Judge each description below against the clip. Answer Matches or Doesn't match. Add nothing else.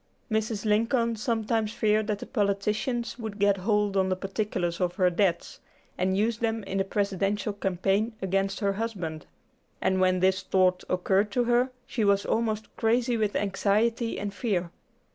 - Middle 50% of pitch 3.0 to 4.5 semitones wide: Doesn't match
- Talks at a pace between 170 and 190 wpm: Doesn't match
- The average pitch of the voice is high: Matches